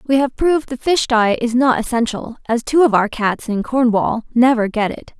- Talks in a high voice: Yes, high, 240 Hz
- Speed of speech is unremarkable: No, fast, 220 wpm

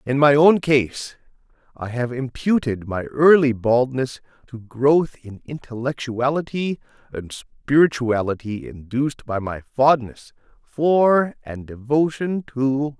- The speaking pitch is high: No, low, 130 Hz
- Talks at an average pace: No, slow, 115 wpm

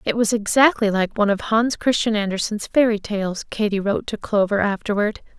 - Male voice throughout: No, female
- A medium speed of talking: Yes, average, 180 wpm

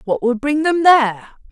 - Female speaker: Yes, female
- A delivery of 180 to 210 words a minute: Yes, average, 200 wpm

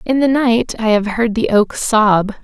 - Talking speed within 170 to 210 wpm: No, fast, 220 wpm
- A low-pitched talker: No, high, 225 Hz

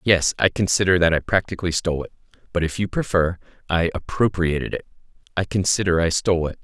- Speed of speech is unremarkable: Yes, average, 180 wpm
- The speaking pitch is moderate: No, very low, 90 Hz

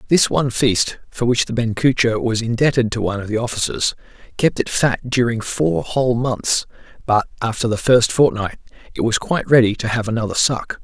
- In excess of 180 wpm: Yes, average, 190 wpm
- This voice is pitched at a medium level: No, low, 120 Hz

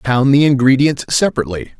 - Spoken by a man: Yes, male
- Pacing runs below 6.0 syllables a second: No, 6.3 syllables/s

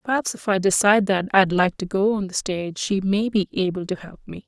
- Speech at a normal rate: No, fast, 255 wpm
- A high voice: Yes, high, 195 Hz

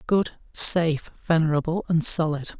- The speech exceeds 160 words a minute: No, slow, 115 wpm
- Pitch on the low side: No, medium, 160 Hz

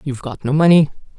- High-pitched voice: No, medium, 145 Hz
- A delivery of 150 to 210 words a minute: Yes, average, 200 wpm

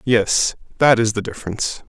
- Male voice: Yes, male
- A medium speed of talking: Yes, average, 155 wpm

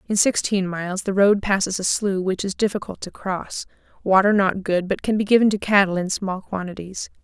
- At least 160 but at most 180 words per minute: No, fast, 205 wpm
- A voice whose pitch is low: No, high, 195 Hz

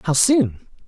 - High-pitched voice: Yes, high, 220 Hz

